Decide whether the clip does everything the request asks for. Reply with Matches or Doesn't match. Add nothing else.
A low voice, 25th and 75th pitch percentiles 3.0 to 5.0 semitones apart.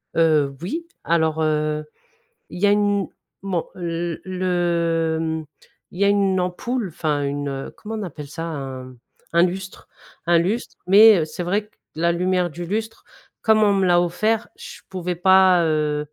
Doesn't match